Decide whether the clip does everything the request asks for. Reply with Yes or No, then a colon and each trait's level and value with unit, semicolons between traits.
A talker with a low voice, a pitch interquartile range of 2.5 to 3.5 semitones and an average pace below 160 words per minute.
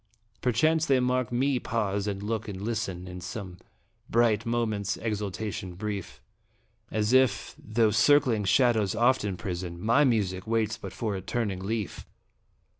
Yes: low, 110 Hz; average, 3.2 semitones; average, 140 wpm